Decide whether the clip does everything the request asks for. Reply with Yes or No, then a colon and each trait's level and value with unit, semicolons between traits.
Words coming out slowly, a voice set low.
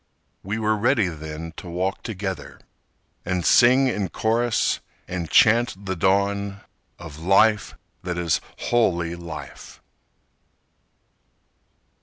Yes: slow, 105 wpm; very low, 95 Hz